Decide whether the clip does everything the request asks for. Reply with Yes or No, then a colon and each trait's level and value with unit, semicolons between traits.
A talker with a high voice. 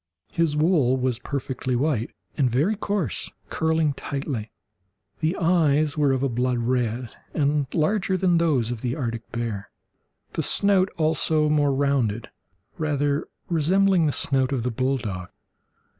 No: medium, 140 Hz